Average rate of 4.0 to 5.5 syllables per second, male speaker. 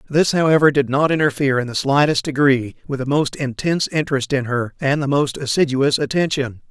No: 5.7 syllables/s; male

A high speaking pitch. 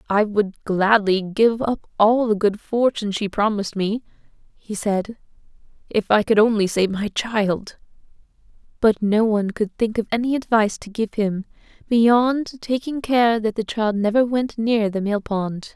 Yes: high, 215 Hz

